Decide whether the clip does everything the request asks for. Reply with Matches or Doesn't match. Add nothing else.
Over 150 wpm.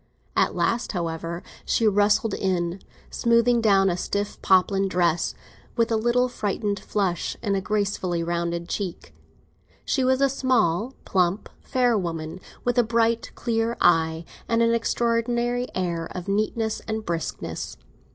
Doesn't match